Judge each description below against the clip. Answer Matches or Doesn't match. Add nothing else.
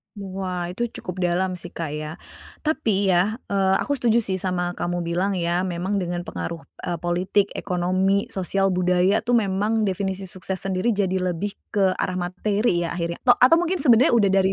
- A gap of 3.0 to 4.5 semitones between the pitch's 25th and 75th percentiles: Doesn't match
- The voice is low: Doesn't match